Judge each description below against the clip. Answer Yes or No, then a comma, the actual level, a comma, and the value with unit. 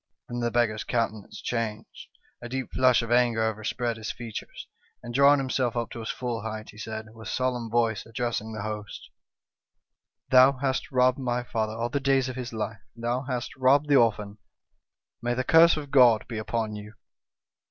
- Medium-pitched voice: No, low, 120 Hz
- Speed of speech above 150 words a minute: Yes, average, 185 wpm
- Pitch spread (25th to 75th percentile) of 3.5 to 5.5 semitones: No, narrow, 2.5 semitones